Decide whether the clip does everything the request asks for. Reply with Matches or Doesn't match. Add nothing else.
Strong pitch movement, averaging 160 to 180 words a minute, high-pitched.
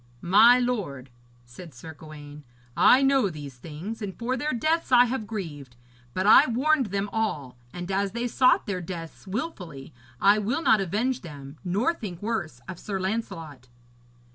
Matches